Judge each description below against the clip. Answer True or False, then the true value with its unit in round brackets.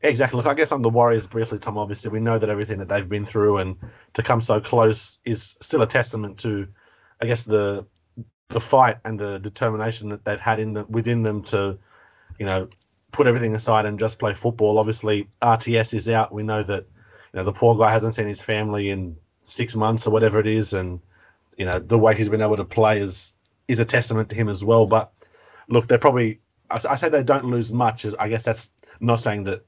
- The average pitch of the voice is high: False (110 Hz)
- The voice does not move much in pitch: True (1.8 semitones)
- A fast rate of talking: True (225 wpm)